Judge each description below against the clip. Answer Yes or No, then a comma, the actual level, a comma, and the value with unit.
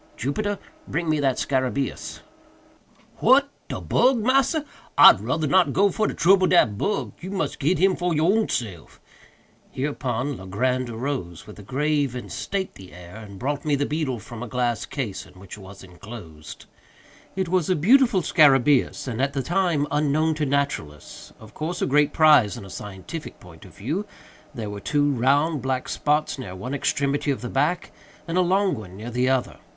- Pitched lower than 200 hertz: Yes, medium, 140 Hz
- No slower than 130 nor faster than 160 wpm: No, average, 175 wpm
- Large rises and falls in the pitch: Yes, wide, 6.2 semitones